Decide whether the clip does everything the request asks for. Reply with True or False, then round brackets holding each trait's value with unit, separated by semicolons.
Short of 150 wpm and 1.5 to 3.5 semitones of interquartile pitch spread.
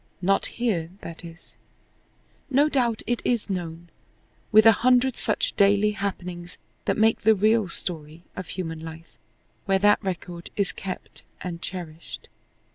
False (140 wpm; 4.2 semitones)